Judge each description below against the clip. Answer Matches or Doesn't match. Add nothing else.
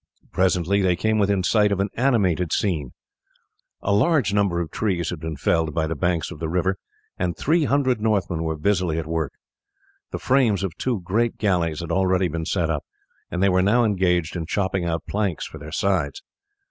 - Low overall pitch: Matches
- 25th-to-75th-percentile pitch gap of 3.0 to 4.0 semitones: Matches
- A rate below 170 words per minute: Doesn't match